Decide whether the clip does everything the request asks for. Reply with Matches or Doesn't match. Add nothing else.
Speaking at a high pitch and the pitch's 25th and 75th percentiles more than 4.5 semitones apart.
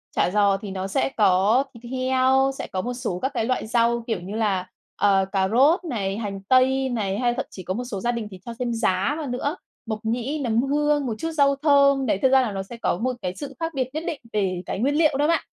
Matches